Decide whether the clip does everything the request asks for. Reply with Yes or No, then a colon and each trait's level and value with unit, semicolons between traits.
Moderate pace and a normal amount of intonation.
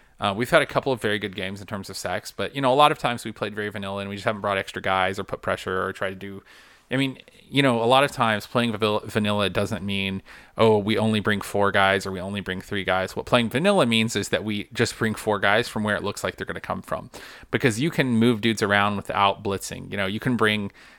No: fast, 275 wpm; average, 3.1 semitones